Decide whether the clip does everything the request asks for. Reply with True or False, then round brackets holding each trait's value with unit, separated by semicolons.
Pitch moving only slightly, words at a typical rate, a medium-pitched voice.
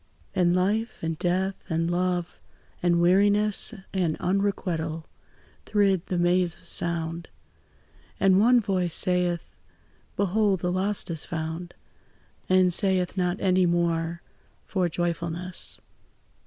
False (1.9 semitones; 115 wpm; 180 Hz)